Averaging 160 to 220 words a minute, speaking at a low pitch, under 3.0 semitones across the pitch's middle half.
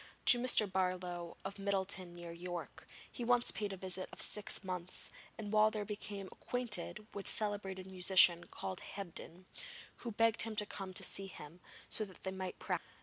No: average, 185 wpm; high, 195 Hz; narrow, 2.5 semitones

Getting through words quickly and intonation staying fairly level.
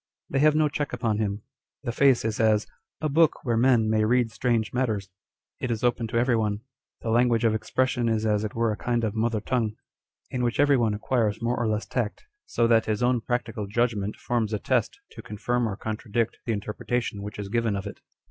Yes: fast, 230 wpm; narrow, 2.2 semitones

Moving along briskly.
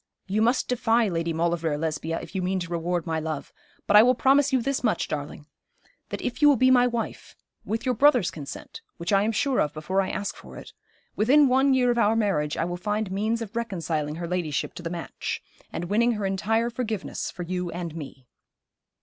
Yes: fast, 215 wpm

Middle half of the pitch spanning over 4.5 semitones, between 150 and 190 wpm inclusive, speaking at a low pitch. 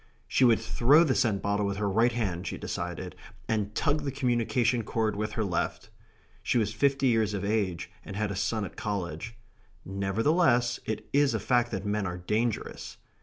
No: average, 3.4 semitones; average, 185 wpm; low, 110 Hz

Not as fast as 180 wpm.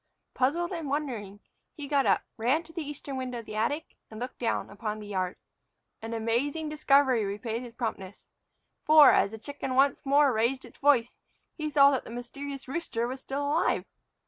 No: average, 185 wpm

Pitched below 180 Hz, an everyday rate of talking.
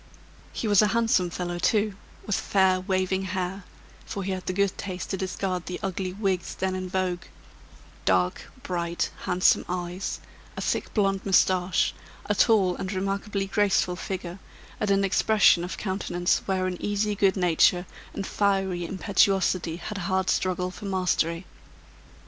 No: high, 190 Hz; average, 150 wpm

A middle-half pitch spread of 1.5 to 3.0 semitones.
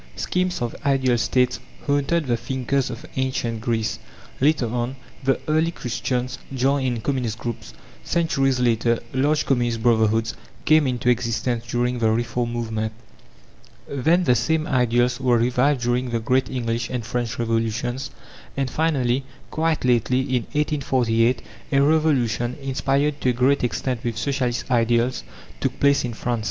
Yes: narrow, 2.5 semitones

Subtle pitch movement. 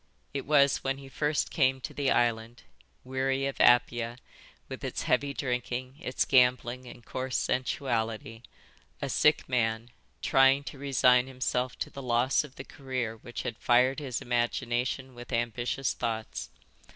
Yes: narrow, 1.9 semitones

